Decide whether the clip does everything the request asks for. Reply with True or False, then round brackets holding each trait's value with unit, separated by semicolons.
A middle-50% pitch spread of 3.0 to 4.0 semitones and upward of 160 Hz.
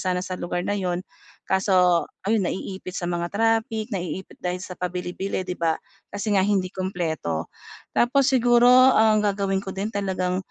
False (2.5 semitones; 190 Hz)